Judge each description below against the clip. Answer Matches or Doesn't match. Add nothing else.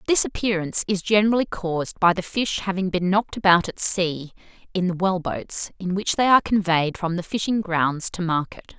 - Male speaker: Doesn't match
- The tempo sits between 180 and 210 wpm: Matches